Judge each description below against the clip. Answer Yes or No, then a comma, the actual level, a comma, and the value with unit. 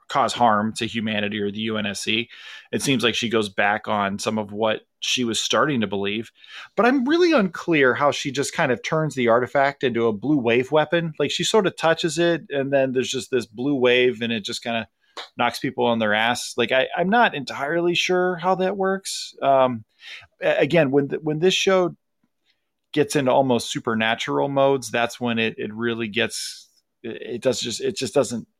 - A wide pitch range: Yes, wide, 6.2 semitones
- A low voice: Yes, low, 130 Hz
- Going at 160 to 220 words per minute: Yes, average, 200 wpm